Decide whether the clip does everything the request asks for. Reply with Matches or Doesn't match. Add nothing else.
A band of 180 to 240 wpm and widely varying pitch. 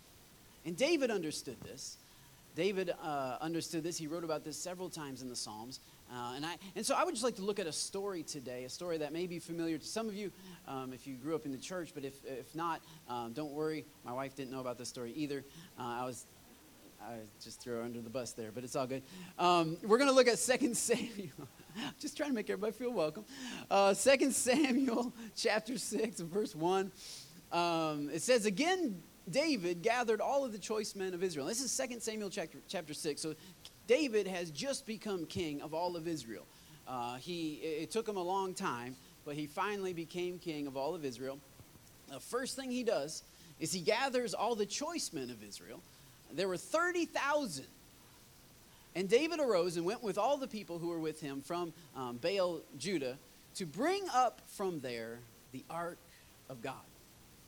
Matches